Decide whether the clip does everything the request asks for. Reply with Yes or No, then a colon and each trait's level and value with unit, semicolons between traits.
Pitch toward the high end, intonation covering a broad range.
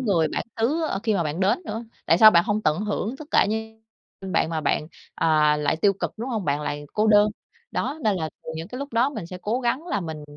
Yes: high, 205 Hz; wide, 5.7 semitones